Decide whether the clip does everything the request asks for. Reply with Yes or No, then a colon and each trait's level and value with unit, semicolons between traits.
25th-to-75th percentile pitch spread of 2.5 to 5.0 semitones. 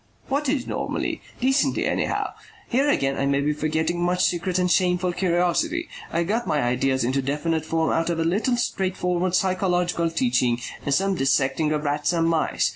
Yes: average, 3.9 semitones